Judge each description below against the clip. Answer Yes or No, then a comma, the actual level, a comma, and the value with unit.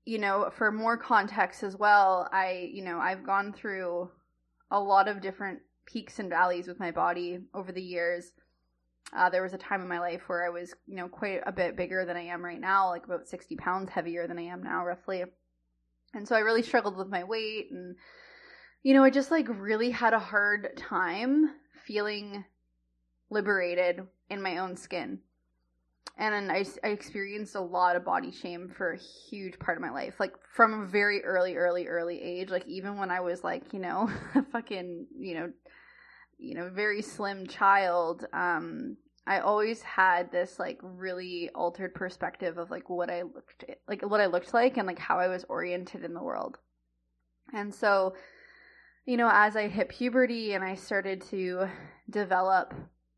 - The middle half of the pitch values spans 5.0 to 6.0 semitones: No, average, 2.8 semitones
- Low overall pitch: No, medium, 185 Hz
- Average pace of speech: Yes, average, 185 wpm